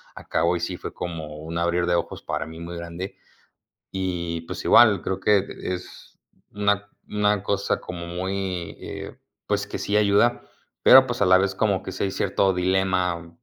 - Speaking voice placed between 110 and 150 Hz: No, very low, 95 Hz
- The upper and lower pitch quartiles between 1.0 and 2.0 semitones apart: No, narrow, 2.6 semitones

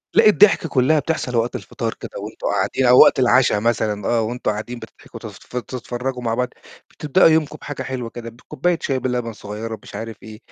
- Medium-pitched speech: No, low, 125 Hz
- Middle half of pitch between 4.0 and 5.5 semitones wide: No, average, 2.7 semitones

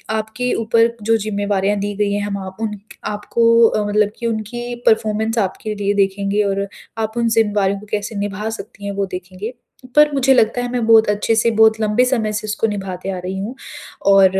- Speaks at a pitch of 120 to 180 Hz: No, high, 210 Hz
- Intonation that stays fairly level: Yes, narrow, 1.9 semitones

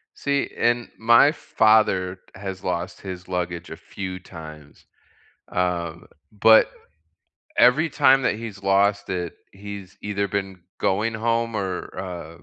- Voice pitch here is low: Yes, very low, 95 Hz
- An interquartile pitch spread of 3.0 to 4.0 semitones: Yes, average, 3.6 semitones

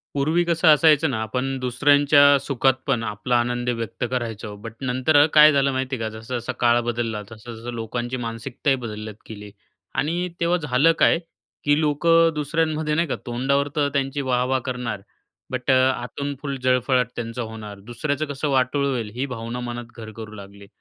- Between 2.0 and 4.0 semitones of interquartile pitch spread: Yes, average, 3.5 semitones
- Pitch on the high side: No, low, 130 Hz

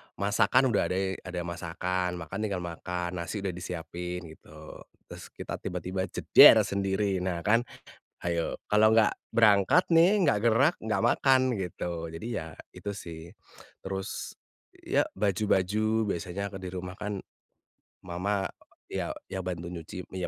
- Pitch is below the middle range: Yes, very low, 95 Hz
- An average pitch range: Yes, average, 3.0 semitones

